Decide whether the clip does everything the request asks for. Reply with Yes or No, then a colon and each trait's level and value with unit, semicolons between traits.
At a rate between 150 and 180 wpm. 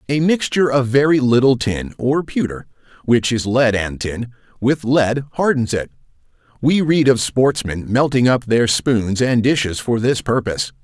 Yes: average, 165 wpm